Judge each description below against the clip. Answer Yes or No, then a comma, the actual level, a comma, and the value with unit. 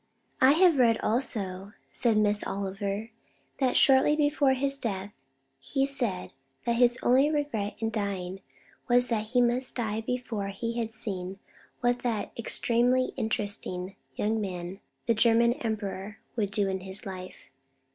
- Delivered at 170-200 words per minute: No, average, 145 wpm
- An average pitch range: Yes, average, 3.7 semitones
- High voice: Yes, high, 225 Hz